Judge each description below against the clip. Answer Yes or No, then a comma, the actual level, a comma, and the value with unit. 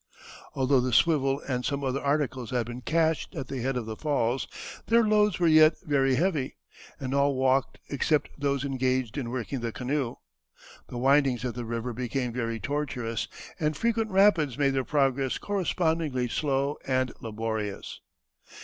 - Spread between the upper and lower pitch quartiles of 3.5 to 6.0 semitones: No, average, 3.1 semitones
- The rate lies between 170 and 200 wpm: No, average, 160 wpm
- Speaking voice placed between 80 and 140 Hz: Yes, low, 135 Hz